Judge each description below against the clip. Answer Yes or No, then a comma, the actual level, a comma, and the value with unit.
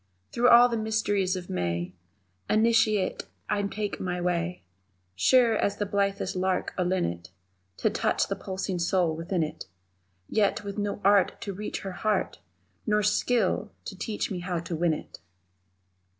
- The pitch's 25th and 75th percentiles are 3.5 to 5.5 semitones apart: No, average, 2.9 semitones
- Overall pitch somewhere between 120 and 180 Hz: No, high, 195 Hz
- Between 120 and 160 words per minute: Yes, average, 155 wpm